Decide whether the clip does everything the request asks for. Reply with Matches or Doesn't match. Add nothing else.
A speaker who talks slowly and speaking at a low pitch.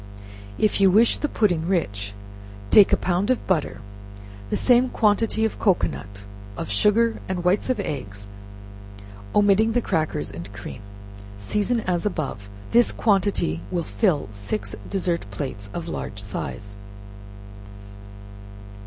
Doesn't match